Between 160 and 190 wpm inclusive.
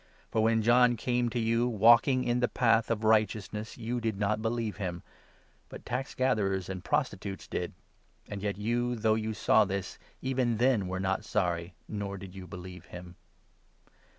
Yes: average, 175 wpm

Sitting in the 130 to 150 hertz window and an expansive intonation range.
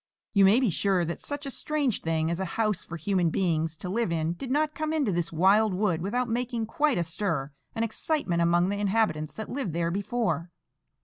No: high, 195 Hz; wide, 5.8 semitones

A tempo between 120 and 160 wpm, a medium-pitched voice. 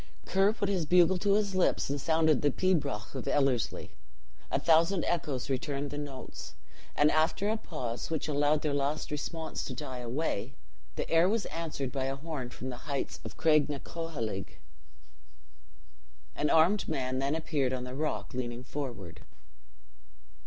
Yes: average, 155 wpm; medium, 145 Hz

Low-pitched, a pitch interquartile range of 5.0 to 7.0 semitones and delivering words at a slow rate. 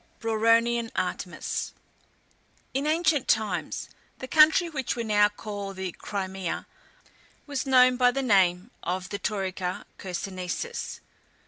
No: high, 215 Hz; average, 5.3 semitones; slow, 115 wpm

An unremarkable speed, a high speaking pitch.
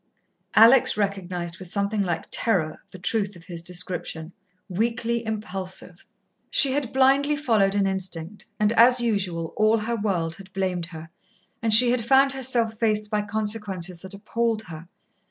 Yes: average, 155 wpm; high, 205 Hz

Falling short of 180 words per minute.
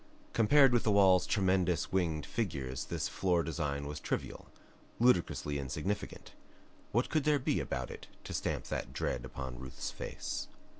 Yes: average, 150 wpm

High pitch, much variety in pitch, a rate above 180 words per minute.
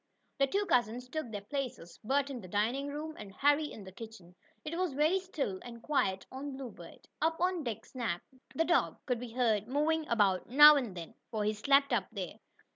Yes: very high, 250 Hz; wide, 5.9 semitones; fast, 205 wpm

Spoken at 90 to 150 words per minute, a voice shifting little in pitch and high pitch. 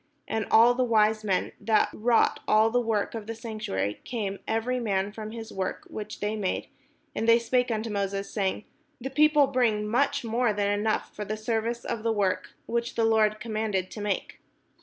No: average, 190 wpm; narrow, 2.0 semitones; high, 220 Hz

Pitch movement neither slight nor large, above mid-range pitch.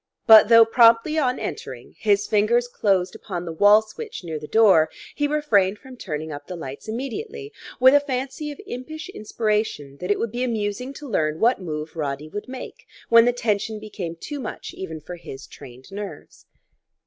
No: wide, 6.4 semitones; high, 215 Hz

